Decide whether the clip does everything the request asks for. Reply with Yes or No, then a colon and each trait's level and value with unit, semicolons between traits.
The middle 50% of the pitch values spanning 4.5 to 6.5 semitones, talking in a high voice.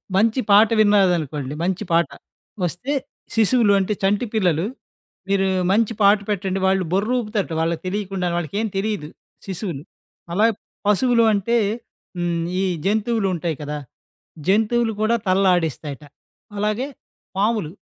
No: average, 3.7 semitones; high, 195 Hz